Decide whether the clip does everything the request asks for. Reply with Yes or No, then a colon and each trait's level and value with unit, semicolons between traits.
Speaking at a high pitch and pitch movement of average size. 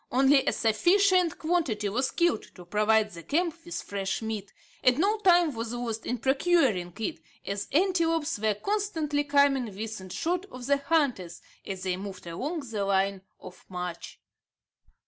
No: very high, 250 Hz; wide, 8.4 semitones